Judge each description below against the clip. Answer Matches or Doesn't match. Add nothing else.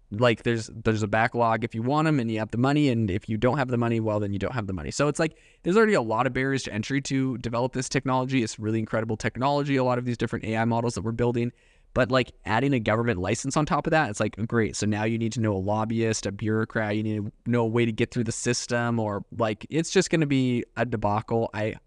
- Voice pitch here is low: Matches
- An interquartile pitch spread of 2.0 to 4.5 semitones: Matches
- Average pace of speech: Doesn't match